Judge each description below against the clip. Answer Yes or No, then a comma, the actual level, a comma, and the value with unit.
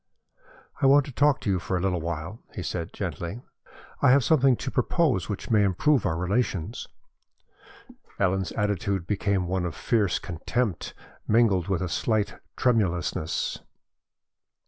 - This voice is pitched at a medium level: No, low, 100 Hz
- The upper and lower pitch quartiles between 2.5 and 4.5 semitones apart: No, average, 5.2 semitones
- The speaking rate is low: No, average, 145 wpm